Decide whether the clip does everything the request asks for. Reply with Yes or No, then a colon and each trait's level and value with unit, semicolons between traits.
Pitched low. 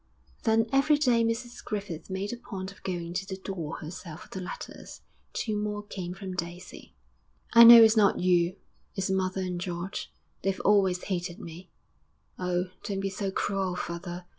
No: high, 190 Hz